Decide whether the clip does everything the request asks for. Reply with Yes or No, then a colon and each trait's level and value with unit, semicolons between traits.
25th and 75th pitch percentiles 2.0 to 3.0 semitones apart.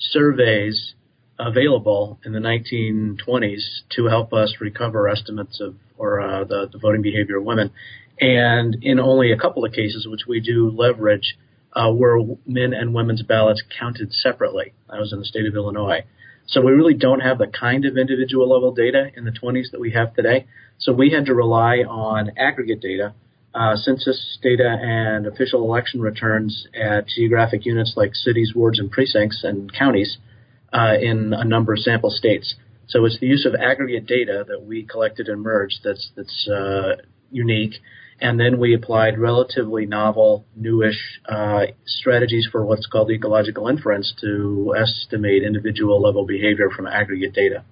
Yes: narrow, 2.5 semitones